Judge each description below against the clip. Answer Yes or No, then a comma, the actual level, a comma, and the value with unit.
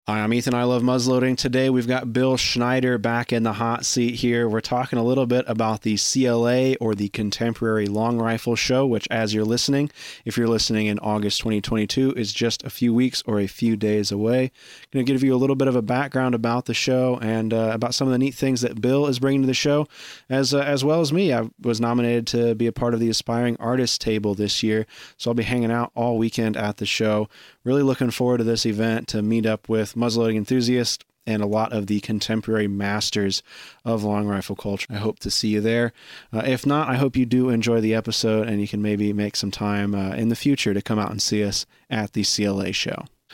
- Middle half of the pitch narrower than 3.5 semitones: Yes, average, 2.8 semitones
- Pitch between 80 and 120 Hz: Yes, low, 115 Hz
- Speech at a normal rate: No, fast, 235 wpm